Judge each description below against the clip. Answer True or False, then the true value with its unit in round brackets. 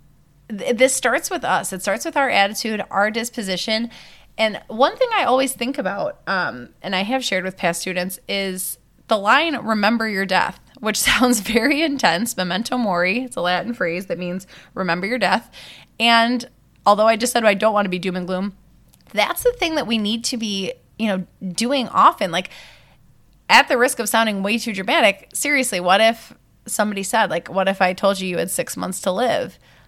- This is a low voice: False (220 Hz)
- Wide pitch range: False (4.8 semitones)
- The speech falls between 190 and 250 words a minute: True (195 wpm)